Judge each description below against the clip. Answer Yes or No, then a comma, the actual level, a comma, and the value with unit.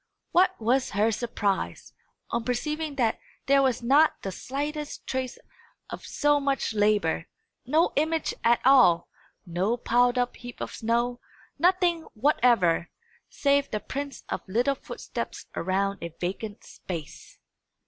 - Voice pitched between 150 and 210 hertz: No, high, 245 Hz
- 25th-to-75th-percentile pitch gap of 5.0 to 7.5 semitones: Yes, average, 5.3 semitones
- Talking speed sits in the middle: No, slow, 130 wpm